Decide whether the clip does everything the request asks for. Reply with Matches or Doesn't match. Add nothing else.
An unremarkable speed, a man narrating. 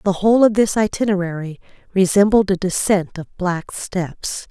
Doesn't match